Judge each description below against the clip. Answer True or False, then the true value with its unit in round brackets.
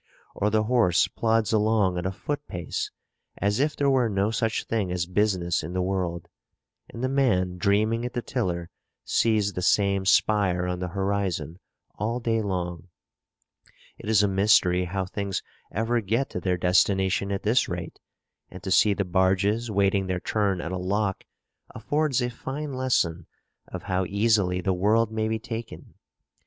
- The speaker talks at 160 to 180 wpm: True (170 wpm)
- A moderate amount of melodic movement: True (3.6 semitones)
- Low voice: True (100 Hz)